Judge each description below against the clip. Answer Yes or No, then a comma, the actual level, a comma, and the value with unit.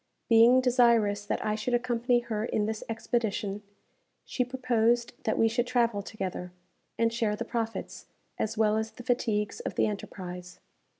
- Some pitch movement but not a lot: No, narrow, 2.3 semitones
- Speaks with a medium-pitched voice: No, high, 225 Hz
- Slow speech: No, average, 160 wpm